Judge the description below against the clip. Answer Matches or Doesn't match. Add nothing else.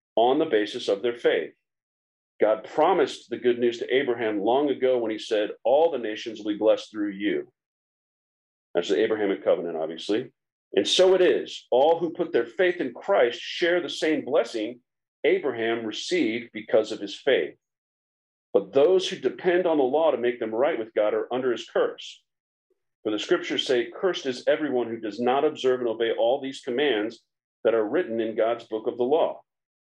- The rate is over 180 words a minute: Matches